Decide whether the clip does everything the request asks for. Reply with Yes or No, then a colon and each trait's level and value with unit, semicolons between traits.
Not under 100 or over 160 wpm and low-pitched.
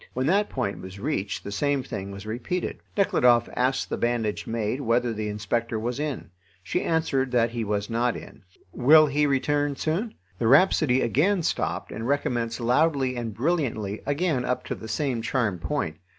No: average, 175 wpm; low, 125 Hz